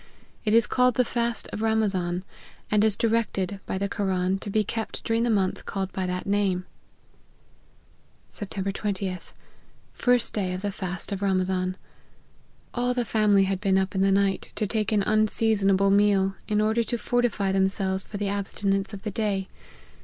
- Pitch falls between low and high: No, high, 200 Hz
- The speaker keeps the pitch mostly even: Yes, narrow, 2.2 semitones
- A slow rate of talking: No, average, 175 wpm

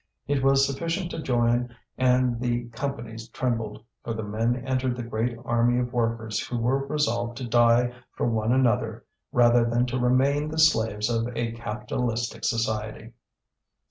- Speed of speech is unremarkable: Yes, average, 155 wpm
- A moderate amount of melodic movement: No, narrow, 2.0 semitones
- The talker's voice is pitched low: Yes, low, 120 Hz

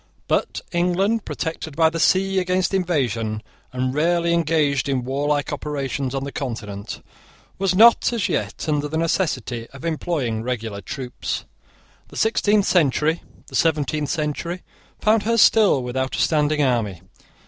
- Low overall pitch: No, medium, 150 Hz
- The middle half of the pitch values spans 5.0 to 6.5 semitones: Yes, average, 5.3 semitones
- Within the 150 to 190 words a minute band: No, average, 140 wpm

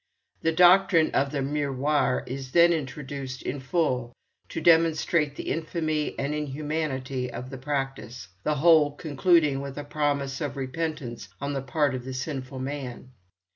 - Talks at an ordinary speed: Yes, average, 150 wpm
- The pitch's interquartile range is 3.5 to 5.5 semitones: No, average, 2.8 semitones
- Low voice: No, medium, 145 Hz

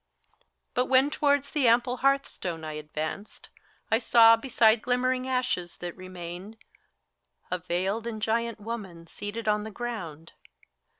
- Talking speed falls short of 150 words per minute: Yes, average, 140 wpm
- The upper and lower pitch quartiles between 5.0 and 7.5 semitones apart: Yes, wide, 5.5 semitones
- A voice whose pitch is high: Yes, high, 220 Hz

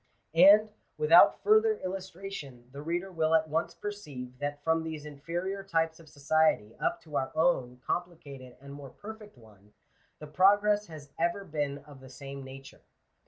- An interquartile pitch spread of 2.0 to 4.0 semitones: No, average, 5.1 semitones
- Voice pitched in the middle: Yes, medium, 155 Hz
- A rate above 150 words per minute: Yes, average, 160 wpm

